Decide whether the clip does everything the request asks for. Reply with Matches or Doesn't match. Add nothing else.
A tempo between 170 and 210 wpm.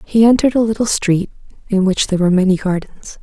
Matches